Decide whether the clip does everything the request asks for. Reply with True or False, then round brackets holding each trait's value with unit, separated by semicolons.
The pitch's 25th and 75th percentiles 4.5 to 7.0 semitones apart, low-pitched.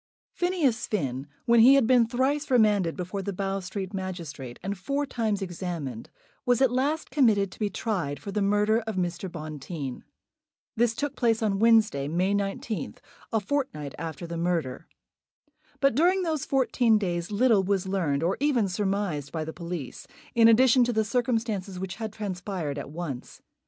False (5.2 semitones; 200 Hz)